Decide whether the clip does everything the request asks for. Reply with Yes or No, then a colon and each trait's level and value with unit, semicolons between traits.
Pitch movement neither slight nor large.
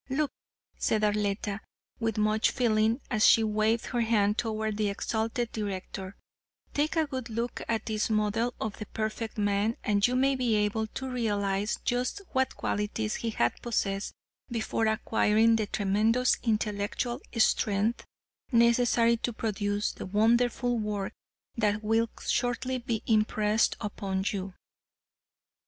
No: narrow, 2.2 semitones